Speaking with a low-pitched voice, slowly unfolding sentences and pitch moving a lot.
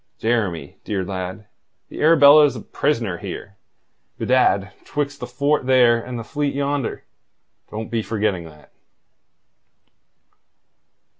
Yes: low, 115 Hz; slow, 115 wpm; wide, 6.0 semitones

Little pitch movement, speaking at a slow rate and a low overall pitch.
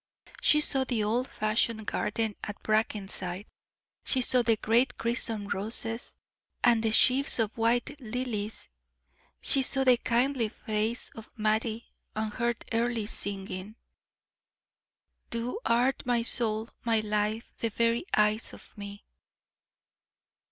No: narrow, 2.0 semitones; slow, 125 wpm; high, 225 Hz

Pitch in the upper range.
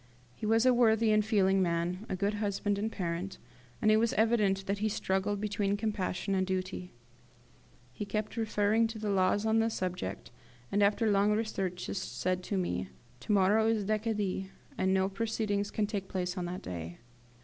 Yes: high, 200 Hz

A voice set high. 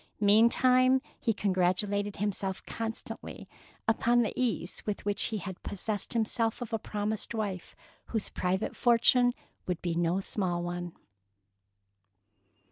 Yes: high, 205 Hz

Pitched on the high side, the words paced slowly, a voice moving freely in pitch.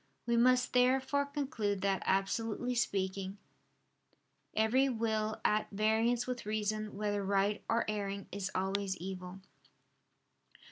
No: high, 215 Hz; slow, 110 wpm; average, 3.1 semitones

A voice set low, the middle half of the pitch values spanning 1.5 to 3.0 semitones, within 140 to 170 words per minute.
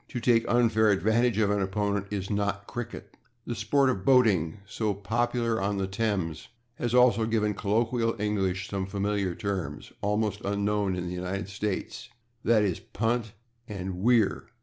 Yes: low, 105 Hz; average, 2.7 semitones; average, 155 wpm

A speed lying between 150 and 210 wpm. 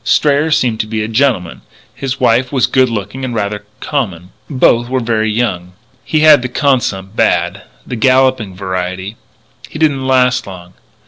Yes: average, 165 wpm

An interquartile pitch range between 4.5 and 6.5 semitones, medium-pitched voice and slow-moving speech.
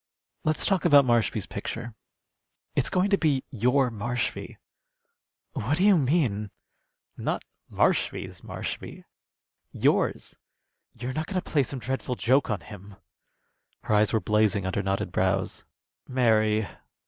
No: average, 5.0 semitones; low, 120 Hz; slow, 130 wpm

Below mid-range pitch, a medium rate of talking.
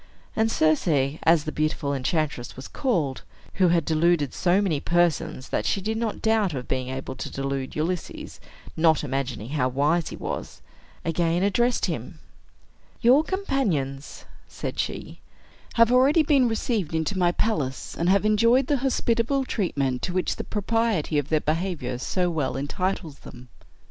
No: medium, 170 Hz; average, 155 wpm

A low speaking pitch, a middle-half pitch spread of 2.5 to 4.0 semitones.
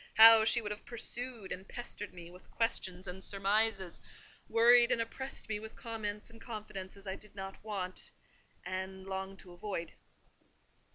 No: high, 205 Hz; average, 3.1 semitones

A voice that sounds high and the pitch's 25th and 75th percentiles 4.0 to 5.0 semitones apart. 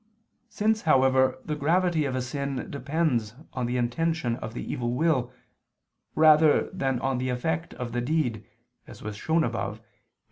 No: low, 135 Hz; average, 4.6 semitones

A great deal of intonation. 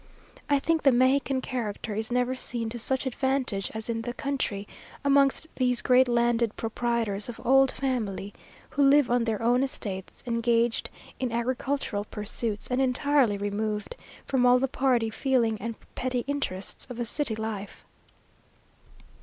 No: average, 3.1 semitones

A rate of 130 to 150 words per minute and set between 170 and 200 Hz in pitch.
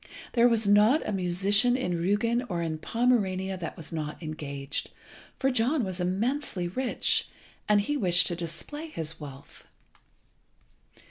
Yes: average, 140 wpm; high, 190 Hz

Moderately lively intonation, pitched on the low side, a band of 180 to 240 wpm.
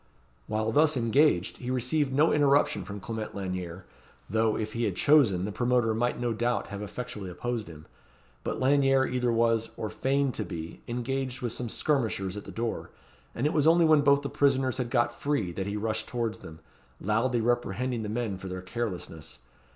Yes: average, 4.1 semitones; low, 120 Hz; average, 190 wpm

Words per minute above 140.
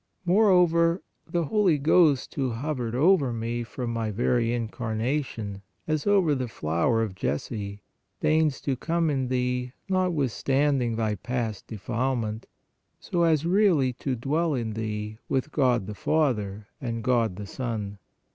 No: slow, 135 wpm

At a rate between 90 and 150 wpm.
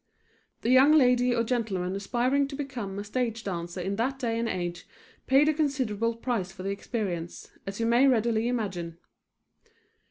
No: average, 165 wpm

